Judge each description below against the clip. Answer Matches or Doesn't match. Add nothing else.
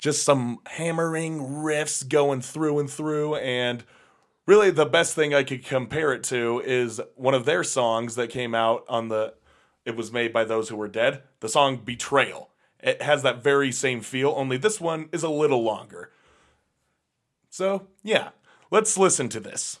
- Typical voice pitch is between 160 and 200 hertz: Doesn't match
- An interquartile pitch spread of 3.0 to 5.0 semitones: Matches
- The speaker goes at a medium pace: Matches